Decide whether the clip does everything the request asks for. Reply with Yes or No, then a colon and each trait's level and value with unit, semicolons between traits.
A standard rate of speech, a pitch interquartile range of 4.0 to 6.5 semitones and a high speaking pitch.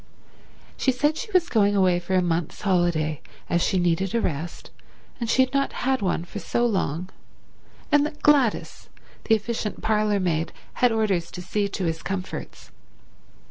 Yes: average, 160 wpm; average, 5.3 semitones; high, 200 Hz